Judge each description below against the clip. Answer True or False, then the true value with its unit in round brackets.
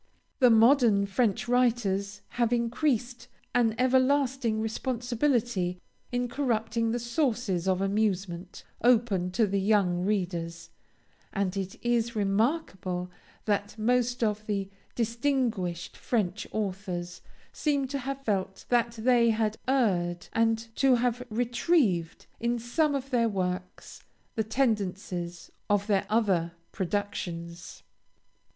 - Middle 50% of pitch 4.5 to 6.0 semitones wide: False (4.0 semitones)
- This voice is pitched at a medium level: False (220 Hz)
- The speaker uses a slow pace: True (115 wpm)